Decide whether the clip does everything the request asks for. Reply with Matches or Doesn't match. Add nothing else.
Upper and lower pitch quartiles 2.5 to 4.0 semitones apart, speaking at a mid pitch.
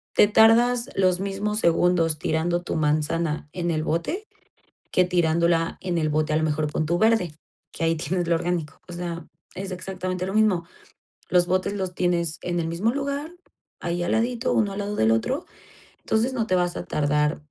Matches